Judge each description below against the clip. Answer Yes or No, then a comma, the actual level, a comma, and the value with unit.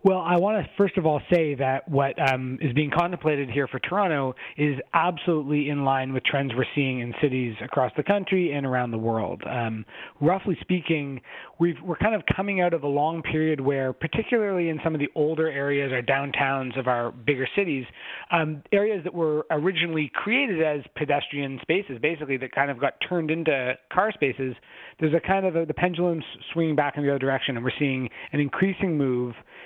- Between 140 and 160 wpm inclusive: No, average, 200 wpm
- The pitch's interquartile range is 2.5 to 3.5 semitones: No, average, 4.3 semitones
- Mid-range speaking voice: Yes, medium, 150 Hz